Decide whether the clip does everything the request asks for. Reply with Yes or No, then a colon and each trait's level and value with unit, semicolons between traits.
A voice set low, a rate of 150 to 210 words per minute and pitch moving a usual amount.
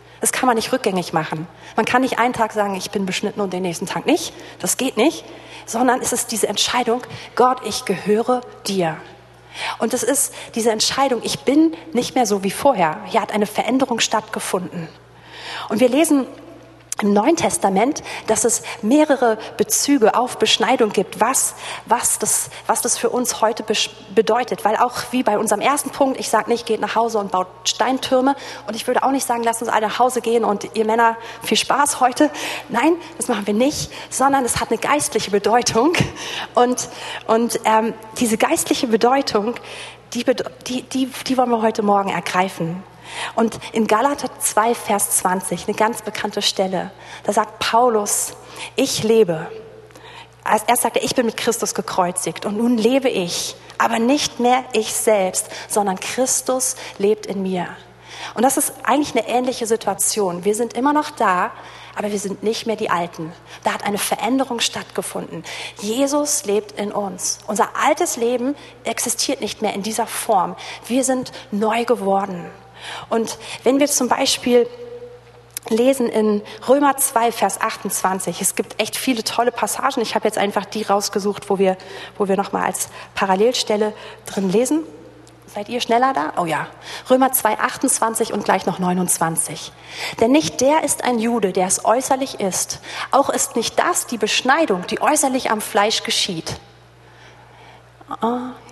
No: high, 225 Hz; average, 170 wpm; average, 3.4 semitones